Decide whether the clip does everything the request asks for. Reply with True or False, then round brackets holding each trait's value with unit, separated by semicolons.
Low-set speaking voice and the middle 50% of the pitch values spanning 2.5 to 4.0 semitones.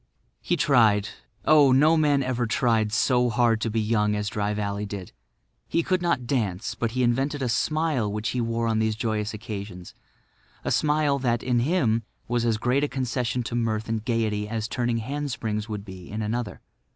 True (115 Hz; 3.2 semitones)